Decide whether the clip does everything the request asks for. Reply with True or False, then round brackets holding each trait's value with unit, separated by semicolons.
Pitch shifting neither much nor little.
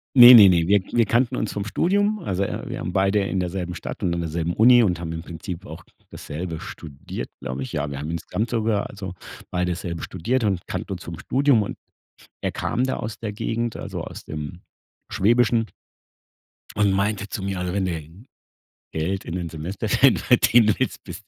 True (4.7 semitones)